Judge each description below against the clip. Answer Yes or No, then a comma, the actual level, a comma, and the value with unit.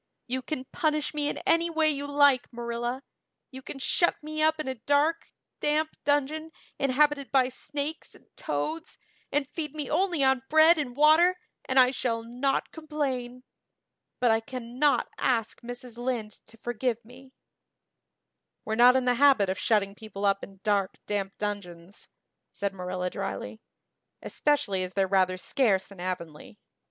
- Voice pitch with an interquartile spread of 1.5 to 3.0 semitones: No, wide, 5.4 semitones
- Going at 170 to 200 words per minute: No, average, 155 wpm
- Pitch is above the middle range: Yes, very high, 255 Hz